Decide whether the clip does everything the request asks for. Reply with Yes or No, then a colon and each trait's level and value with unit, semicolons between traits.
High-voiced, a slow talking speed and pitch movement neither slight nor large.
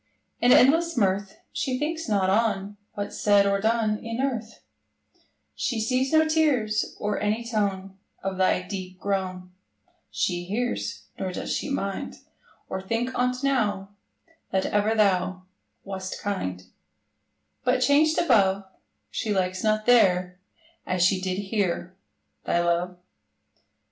Yes: high, 205 Hz; slow, 130 wpm; average, 4.3 semitones